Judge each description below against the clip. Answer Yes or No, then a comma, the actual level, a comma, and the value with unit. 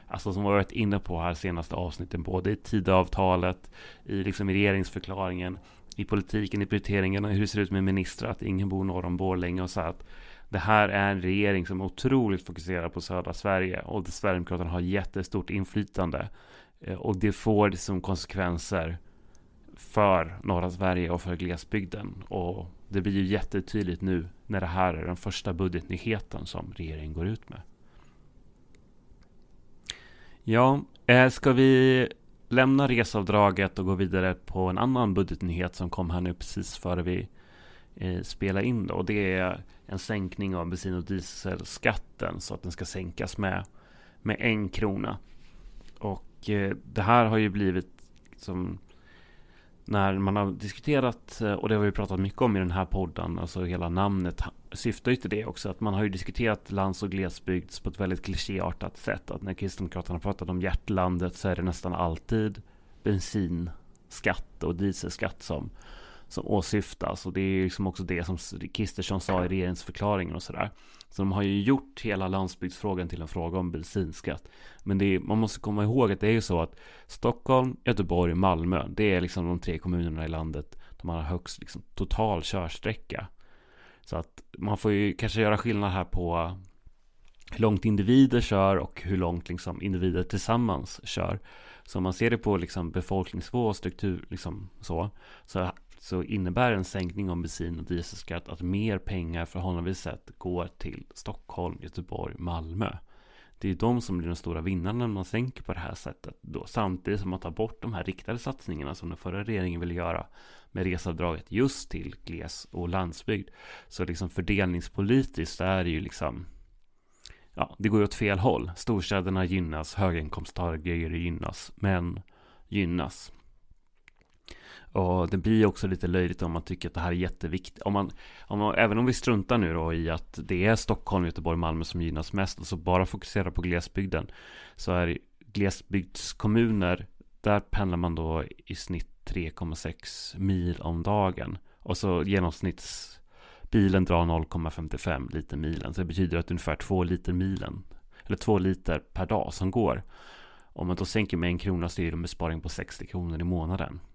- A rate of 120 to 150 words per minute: No, average, 175 wpm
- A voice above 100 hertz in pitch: No, very low, 95 Hz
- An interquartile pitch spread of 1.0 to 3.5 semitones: Yes, narrow, 2.5 semitones